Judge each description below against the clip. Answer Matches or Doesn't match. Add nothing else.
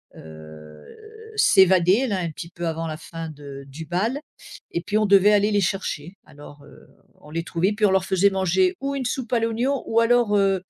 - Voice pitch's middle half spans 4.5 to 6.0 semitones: Matches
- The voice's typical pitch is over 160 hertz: Matches